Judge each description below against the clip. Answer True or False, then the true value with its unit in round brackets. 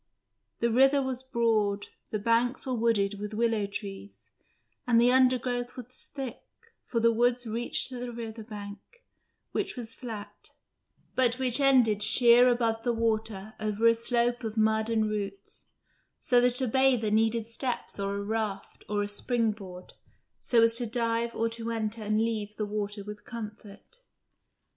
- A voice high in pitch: True (230 Hz)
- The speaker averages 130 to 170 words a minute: True (160 wpm)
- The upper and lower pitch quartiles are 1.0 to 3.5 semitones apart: True (2.4 semitones)